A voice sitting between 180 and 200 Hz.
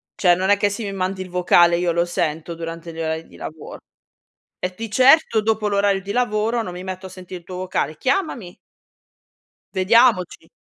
Yes: medium, 185 Hz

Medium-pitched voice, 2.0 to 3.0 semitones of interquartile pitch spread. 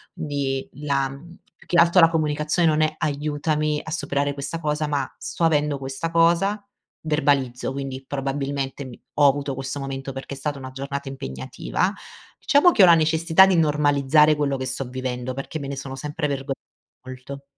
Yes: medium, 145 Hz; narrow, 2.4 semitones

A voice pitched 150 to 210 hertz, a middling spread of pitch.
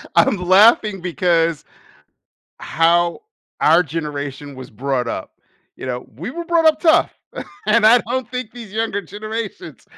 No: medium, 185 Hz; wide, 6.9 semitones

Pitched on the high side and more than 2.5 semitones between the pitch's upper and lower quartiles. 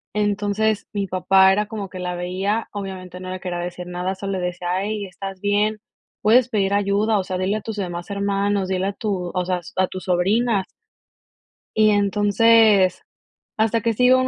No: high, 200 Hz; narrow, 2.2 semitones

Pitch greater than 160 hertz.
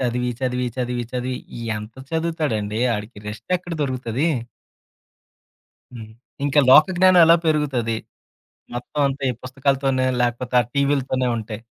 No: low, 130 Hz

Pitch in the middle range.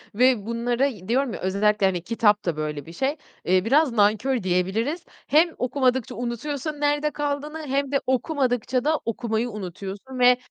No: high, 245 Hz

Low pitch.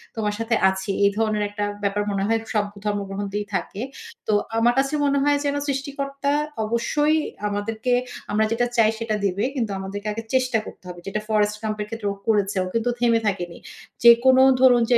No: high, 220 Hz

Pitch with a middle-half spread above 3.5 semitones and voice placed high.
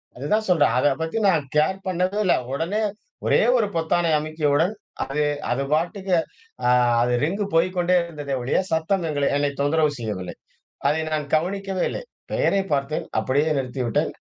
No: average, 4.3 semitones; medium, 160 Hz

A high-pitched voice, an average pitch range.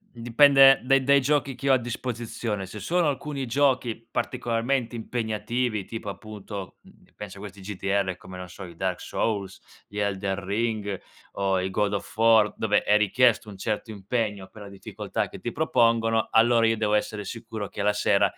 No: low, 110 Hz; average, 3.1 semitones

